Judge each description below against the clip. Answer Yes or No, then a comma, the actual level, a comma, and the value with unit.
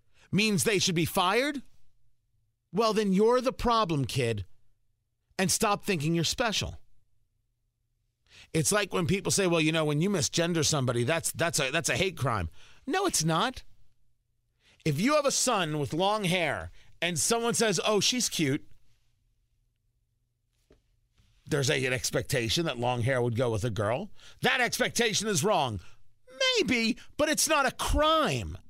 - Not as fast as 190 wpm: Yes, average, 155 wpm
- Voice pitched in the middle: Yes, medium, 150 Hz